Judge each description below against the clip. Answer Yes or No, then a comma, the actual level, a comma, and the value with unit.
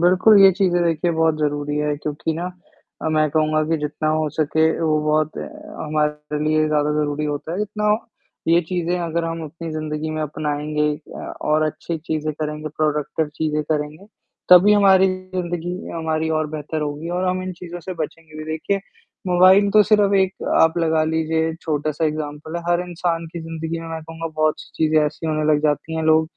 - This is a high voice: No, medium, 160 Hz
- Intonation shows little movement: Yes, narrow, 2.0 semitones